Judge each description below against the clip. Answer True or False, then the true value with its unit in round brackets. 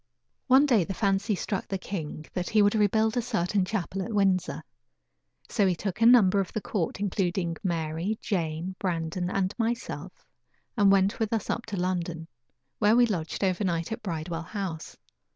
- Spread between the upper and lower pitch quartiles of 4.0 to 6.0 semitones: False (3.6 semitones)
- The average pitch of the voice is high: True (195 Hz)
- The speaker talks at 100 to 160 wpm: False (175 wpm)